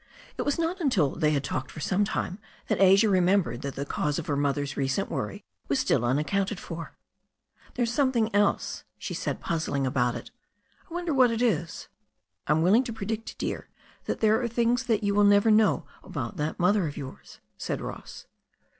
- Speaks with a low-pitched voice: No, high, 195 Hz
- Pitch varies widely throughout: Yes, wide, 7.3 semitones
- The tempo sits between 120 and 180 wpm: No, average, 190 wpm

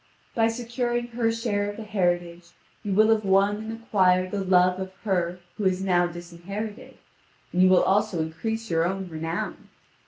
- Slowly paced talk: No, average, 175 wpm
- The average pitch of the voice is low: No, high, 195 Hz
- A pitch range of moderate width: Yes, average, 3.7 semitones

